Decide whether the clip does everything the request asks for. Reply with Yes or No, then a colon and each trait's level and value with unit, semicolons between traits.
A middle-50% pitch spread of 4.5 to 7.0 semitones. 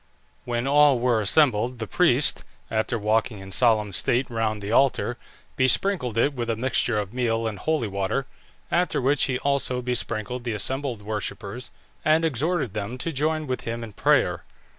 No: average, 3.8 semitones